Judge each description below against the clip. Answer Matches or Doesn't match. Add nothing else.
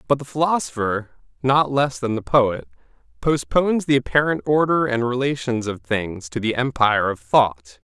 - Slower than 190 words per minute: Matches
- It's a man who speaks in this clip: Matches